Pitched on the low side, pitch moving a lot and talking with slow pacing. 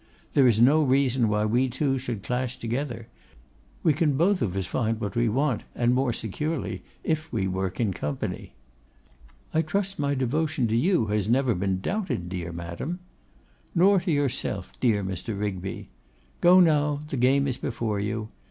No: low, 125 Hz; wide, 5.7 semitones; average, 170 wpm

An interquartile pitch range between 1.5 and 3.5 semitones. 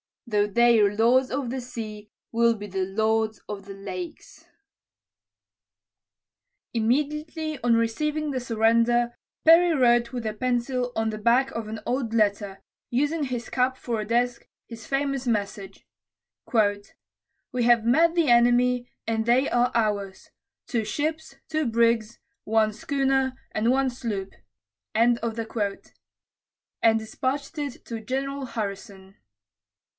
Yes: average, 3.1 semitones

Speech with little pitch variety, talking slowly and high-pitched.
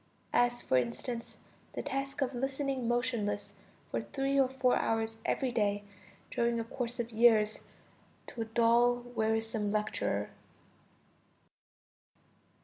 Yes: narrow, 2.3 semitones; slow, 120 wpm; high, 235 Hz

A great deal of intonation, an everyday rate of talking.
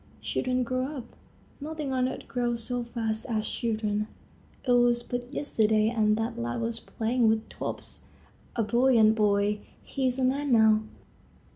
No: narrow, 2.6 semitones; average, 155 wpm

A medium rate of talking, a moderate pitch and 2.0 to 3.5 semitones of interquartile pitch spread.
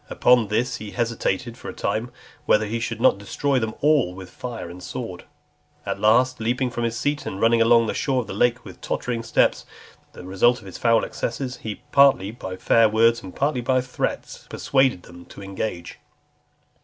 No: average, 190 wpm; low, 115 Hz; average, 3.2 semitones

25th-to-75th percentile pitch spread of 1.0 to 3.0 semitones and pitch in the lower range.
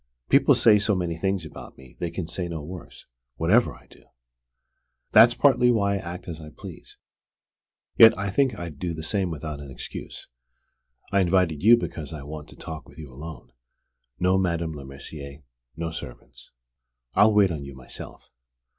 No: average, 4.3 semitones; very low, 85 Hz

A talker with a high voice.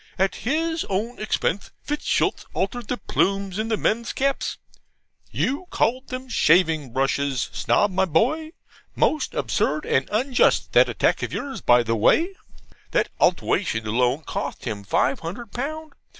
Yes: high, 205 Hz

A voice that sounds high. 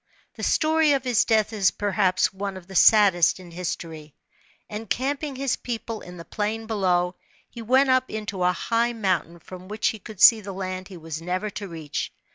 Yes: high, 205 Hz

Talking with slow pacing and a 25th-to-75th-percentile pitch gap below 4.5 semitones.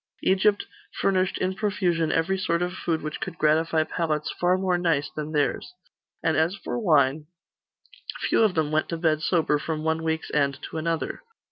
No: average, 175 wpm; average, 2.9 semitones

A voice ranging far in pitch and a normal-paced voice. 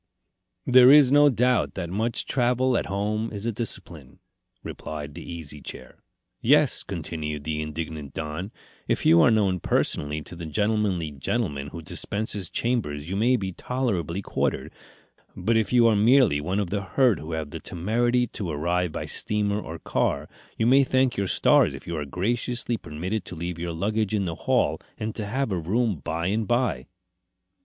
Yes: wide, 6.2 semitones; average, 180 wpm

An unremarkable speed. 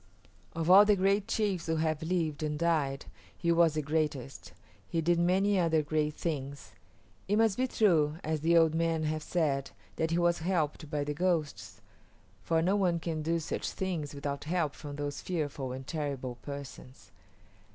Yes: average, 175 wpm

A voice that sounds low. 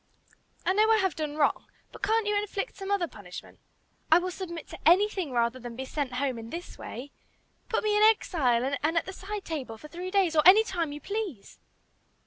No: very high, 340 Hz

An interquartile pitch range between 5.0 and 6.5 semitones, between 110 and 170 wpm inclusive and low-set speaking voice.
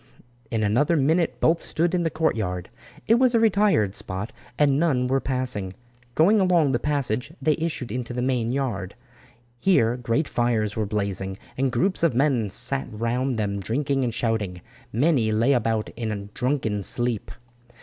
Yes: wide, 5.4 semitones; average, 160 wpm; low, 125 Hz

